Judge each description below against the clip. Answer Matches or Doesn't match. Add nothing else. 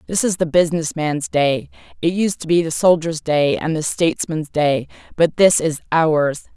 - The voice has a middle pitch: Matches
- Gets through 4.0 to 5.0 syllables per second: Matches